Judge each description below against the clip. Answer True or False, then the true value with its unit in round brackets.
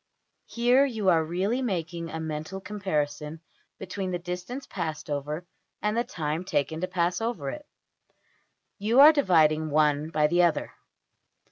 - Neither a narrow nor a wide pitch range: True (4.9 semitones)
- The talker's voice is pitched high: False (175 Hz)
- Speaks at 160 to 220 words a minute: False (150 wpm)